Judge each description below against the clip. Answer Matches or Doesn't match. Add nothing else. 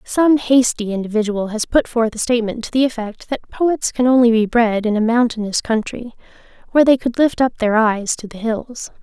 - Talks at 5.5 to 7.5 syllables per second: Doesn't match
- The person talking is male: Doesn't match